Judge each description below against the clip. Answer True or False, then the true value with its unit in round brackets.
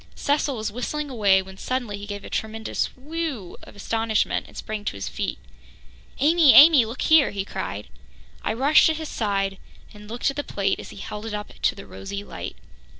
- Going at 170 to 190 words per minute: False (200 wpm)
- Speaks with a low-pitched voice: False (220 Hz)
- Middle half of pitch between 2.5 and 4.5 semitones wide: False (5.6 semitones)